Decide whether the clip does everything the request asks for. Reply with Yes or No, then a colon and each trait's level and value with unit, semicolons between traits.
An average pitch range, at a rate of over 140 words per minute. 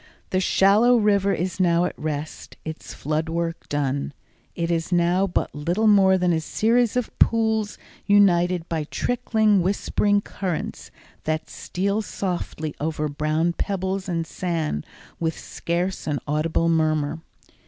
No: average, 3.9 semitones; slow, 135 wpm